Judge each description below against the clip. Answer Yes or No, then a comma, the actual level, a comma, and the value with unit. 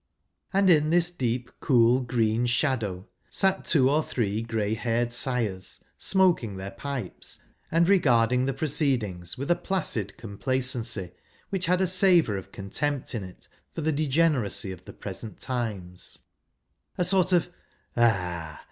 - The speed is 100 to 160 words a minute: Yes, average, 150 wpm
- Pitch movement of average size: No, wide, 6.8 semitones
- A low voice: Yes, low, 125 Hz